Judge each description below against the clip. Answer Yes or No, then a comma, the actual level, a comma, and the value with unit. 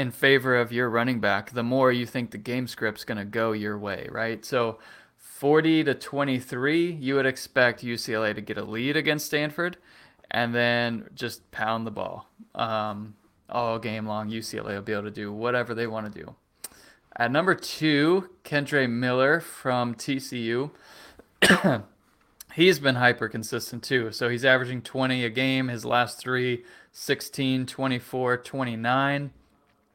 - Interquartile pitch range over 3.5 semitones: No, average, 2.8 semitones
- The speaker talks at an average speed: Yes, average, 150 wpm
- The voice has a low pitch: Yes, low, 125 Hz